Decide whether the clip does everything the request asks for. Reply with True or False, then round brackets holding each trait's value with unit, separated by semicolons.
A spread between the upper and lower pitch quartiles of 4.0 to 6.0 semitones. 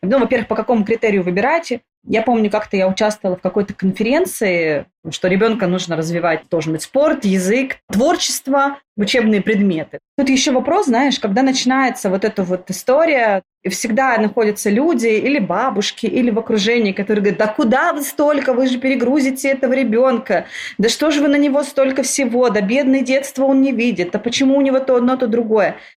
True (4.6 semitones)